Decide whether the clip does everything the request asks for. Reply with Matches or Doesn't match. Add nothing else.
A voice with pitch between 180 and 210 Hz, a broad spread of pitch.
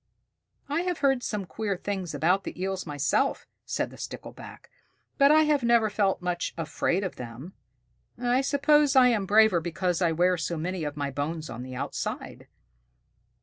Matches